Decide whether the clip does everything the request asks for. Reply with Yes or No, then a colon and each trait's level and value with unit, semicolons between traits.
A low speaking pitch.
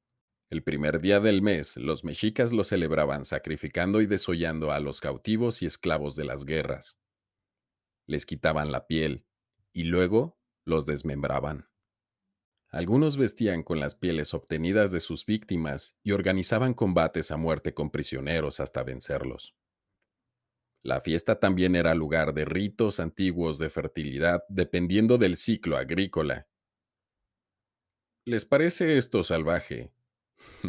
Yes: very low, 90 Hz